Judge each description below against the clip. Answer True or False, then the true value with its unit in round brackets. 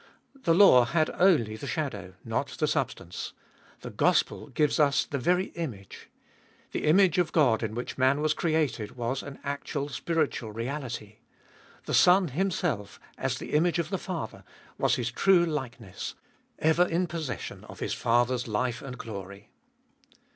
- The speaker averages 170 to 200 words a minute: False (155 wpm)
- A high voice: False (140 Hz)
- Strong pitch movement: True (6.0 semitones)